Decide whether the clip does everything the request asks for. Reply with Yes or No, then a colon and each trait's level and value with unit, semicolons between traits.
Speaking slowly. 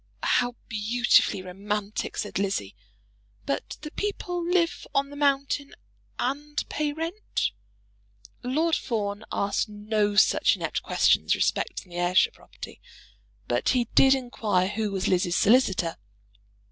Yes: slow, 120 wpm